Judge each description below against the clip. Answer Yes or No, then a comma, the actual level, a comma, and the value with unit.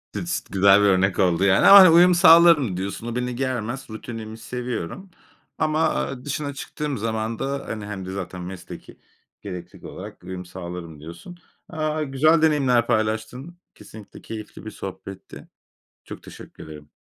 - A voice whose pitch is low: Yes, low, 115 Hz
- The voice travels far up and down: Yes, wide, 7.0 semitones